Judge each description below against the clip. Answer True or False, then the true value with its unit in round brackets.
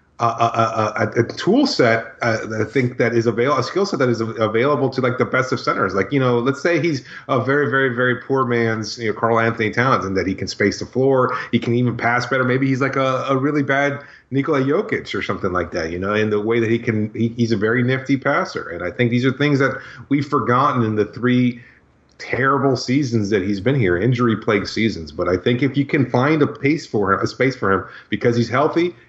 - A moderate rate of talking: False (250 wpm)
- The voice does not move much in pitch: False (3.1 semitones)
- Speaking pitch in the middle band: False (125 Hz)